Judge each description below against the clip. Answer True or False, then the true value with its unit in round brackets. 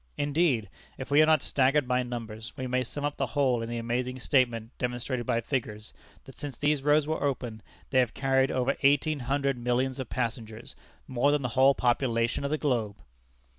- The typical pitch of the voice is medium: False (130 Hz)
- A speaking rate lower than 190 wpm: False (195 wpm)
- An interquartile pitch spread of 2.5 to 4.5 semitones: True (2.9 semitones)